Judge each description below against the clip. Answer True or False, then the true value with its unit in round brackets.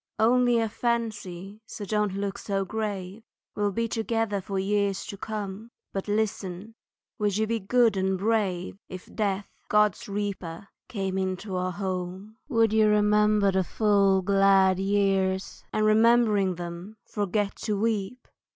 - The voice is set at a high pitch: True (205 Hz)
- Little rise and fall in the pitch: True (2.1 semitones)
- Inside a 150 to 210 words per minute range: False (140 wpm)